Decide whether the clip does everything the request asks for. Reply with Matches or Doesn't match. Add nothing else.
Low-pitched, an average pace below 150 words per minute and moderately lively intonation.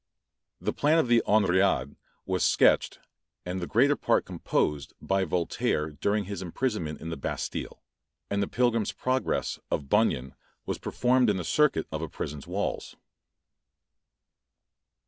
Doesn't match